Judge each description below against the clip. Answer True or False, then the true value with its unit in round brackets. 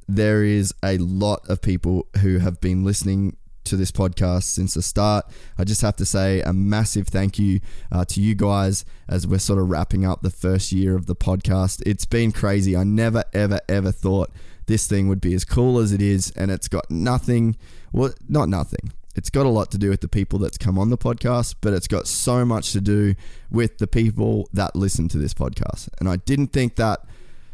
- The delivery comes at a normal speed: False (215 wpm)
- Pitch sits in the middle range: False (100 Hz)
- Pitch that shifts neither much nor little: False (2.3 semitones)